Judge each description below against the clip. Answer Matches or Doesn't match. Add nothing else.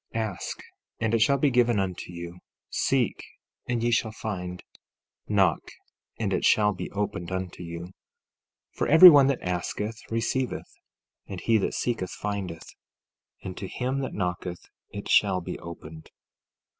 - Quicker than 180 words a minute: Doesn't match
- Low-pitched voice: Matches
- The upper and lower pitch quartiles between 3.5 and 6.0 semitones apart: Matches